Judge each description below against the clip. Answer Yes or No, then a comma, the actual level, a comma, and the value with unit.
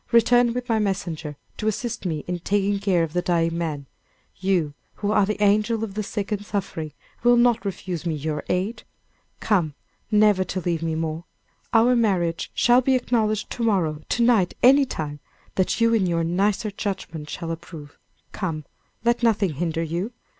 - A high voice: Yes, high, 195 Hz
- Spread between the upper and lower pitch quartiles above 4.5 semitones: Yes, average, 4.9 semitones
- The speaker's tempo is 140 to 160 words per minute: No, average, 175 wpm